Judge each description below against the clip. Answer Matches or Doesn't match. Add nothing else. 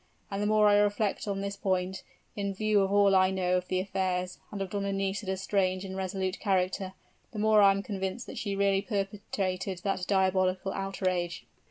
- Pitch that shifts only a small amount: Matches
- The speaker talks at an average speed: Matches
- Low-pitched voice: Doesn't match